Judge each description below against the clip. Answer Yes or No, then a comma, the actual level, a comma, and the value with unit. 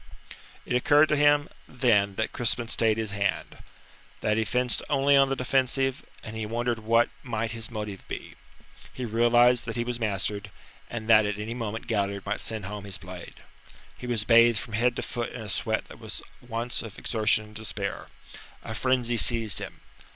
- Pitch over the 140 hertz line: No, low, 115 Hz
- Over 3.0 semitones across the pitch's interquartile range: No, narrow, 2.4 semitones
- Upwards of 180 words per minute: Yes, average, 190 wpm